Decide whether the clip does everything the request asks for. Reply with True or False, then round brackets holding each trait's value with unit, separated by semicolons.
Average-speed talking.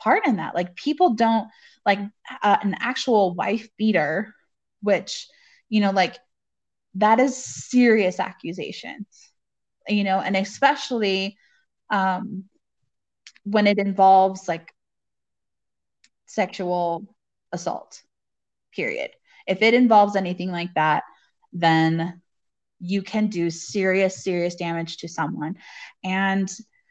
False (105 wpm)